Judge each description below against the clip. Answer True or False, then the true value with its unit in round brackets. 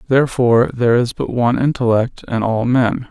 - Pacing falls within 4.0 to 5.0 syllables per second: False (5.6 syllables/s)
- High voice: False (120 Hz)